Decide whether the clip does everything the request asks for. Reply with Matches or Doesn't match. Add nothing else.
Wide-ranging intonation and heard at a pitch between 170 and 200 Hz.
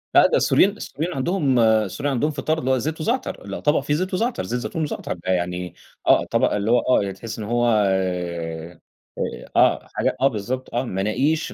Doesn't match